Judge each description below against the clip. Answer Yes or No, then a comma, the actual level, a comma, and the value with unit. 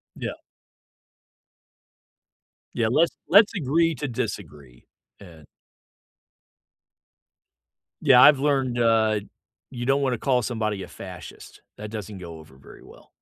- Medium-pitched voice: No, low, 120 Hz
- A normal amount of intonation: Yes, average, 4.8 semitones